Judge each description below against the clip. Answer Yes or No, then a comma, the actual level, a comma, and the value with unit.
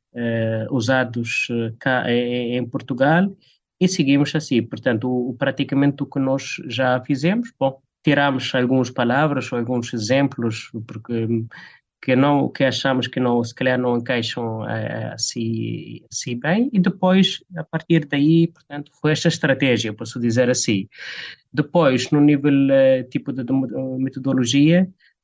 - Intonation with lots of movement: No, average, 3.2 semitones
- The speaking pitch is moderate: No, low, 130 Hz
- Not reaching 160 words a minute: Yes, average, 140 wpm